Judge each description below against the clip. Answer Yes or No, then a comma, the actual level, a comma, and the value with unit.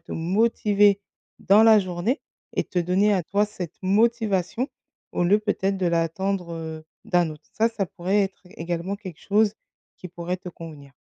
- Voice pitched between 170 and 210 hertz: Yes, high, 190 Hz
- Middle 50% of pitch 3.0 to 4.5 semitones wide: Yes, average, 3.3 semitones